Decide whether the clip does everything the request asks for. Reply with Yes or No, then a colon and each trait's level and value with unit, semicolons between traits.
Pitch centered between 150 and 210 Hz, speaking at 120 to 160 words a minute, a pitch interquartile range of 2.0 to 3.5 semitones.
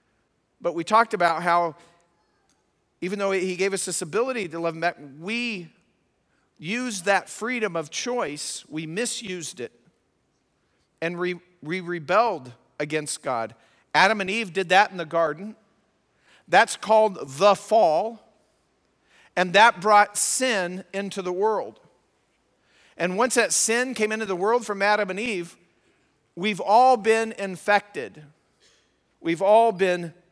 No: high, 190 Hz; slow, 135 wpm; average, 4.3 semitones